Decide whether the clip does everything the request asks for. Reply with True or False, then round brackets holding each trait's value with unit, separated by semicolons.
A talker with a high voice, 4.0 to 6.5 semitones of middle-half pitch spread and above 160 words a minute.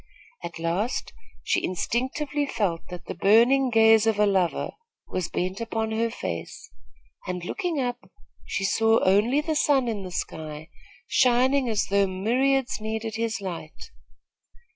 False (220 Hz; 5.1 semitones; 140 wpm)